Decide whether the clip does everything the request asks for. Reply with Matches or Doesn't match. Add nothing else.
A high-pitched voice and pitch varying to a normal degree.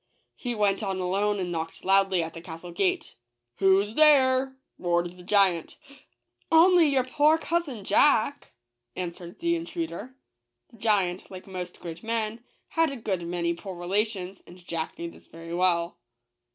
Doesn't match